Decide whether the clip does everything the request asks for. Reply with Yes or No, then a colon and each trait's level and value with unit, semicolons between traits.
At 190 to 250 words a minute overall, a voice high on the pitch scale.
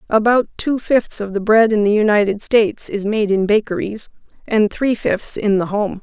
Yes: average, 200 wpm; high, 210 Hz